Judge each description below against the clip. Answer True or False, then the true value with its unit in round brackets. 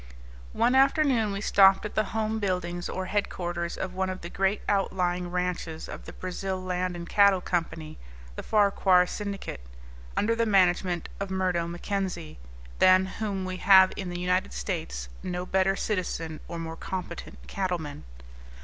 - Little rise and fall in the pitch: True (2.1 semitones)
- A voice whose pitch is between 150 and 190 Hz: True (185 Hz)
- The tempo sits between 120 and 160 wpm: True (155 wpm)